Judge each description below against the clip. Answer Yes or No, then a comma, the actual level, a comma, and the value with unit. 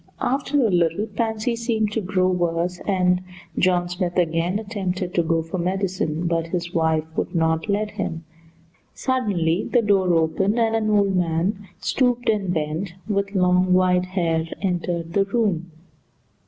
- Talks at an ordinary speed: Yes, average, 155 wpm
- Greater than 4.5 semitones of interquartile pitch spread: No, average, 3.3 semitones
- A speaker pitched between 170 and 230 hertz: Yes, medium, 185 Hz